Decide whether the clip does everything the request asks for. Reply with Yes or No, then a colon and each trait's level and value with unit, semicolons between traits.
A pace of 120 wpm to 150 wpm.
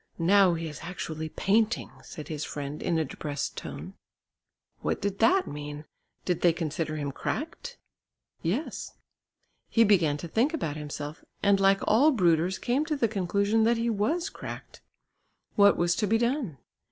No: average, 160 wpm